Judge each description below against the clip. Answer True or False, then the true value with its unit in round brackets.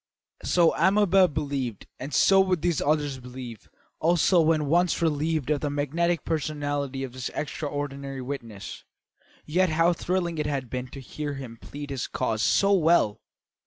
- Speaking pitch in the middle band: True (145 Hz)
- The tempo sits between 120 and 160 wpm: True (155 wpm)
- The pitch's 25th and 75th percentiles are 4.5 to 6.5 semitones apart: False (3.8 semitones)